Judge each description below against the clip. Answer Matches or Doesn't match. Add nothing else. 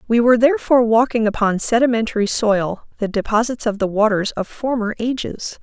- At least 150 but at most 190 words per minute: Matches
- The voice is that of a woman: Matches